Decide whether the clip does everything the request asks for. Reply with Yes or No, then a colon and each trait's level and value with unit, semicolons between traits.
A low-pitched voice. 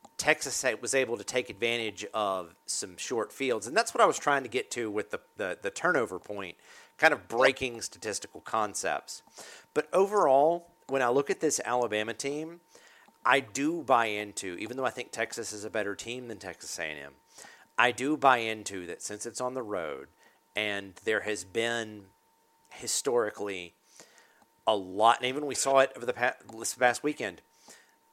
Yes: low, 120 Hz